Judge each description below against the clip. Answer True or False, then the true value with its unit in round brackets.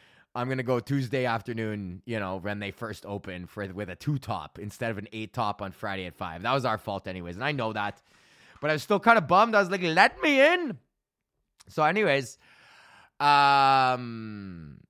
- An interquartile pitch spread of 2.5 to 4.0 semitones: False (5.6 semitones)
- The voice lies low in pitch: True (115 Hz)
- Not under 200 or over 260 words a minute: True (205 wpm)